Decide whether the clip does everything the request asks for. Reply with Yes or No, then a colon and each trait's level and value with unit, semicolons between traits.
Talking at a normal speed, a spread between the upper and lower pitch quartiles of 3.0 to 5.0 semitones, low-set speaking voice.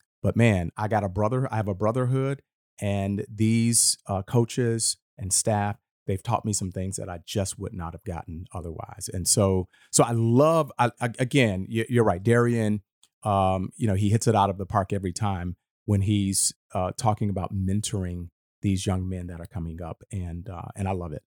Yes: average, 195 wpm; average, 3.4 semitones; low, 100 Hz